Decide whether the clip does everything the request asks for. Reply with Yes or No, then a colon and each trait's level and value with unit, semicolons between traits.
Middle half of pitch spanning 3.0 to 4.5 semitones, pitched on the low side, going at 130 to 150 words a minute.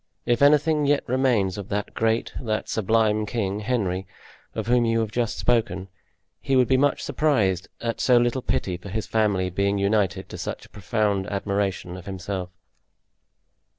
No: average, 3.6 semitones; low, 110 Hz; average, 165 wpm